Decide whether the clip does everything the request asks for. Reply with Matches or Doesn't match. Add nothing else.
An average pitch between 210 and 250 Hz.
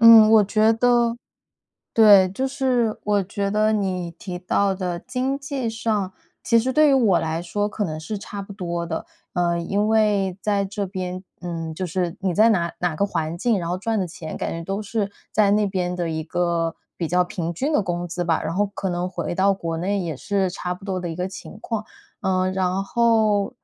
Doesn't match